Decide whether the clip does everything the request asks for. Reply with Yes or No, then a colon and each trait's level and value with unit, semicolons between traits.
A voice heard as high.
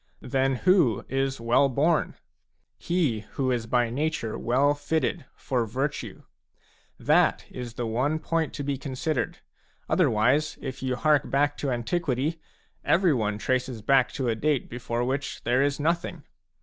No: low, 135 Hz